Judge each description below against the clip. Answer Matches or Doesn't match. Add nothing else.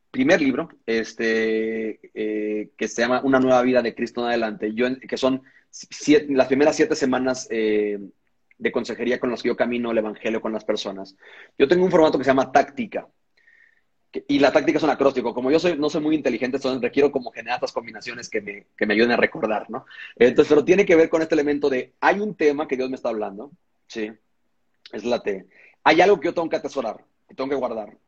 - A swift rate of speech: Matches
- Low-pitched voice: Matches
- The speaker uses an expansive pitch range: Matches